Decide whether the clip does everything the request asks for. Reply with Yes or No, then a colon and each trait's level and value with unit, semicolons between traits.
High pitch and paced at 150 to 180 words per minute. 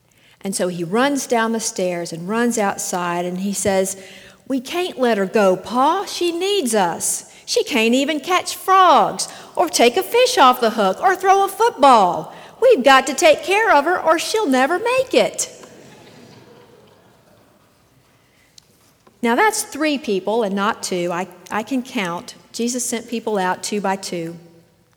Yes: high, 235 Hz; average, 165 wpm